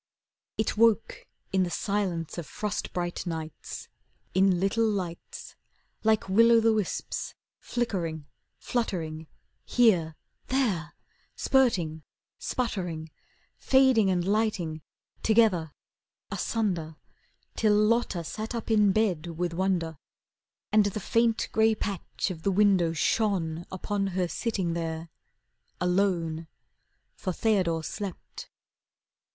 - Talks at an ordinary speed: No, slow, 110 wpm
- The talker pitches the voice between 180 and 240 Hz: Yes, high, 190 Hz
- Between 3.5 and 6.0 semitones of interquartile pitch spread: Yes, average, 4.5 semitones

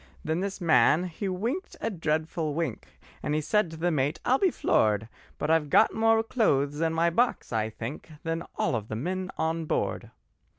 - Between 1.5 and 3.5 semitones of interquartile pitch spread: No, average, 4.4 semitones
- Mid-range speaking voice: Yes, medium, 165 Hz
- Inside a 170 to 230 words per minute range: Yes, average, 185 wpm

